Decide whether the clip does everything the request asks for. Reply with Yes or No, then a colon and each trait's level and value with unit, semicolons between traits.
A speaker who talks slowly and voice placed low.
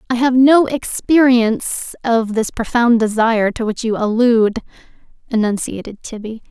No: slow, 130 wpm; high, 230 Hz